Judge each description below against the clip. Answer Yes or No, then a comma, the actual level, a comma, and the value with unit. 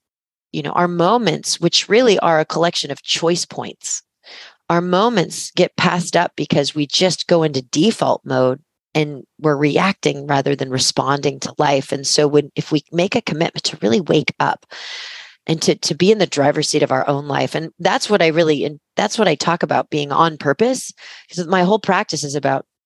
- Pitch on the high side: No, medium, 155 Hz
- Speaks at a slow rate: No, average, 200 wpm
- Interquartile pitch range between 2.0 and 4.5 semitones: Yes, average, 3.6 semitones